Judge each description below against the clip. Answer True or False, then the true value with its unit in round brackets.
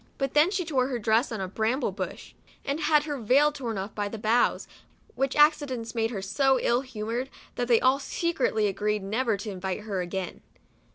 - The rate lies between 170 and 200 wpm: True (195 wpm)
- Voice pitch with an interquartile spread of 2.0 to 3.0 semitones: False (4.6 semitones)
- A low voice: False (235 Hz)